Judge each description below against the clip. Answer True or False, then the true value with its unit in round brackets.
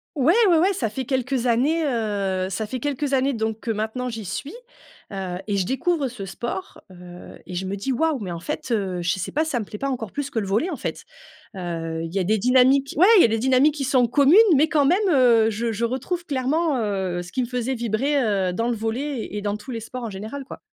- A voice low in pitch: False (235 Hz)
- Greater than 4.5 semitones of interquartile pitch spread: True (5.1 semitones)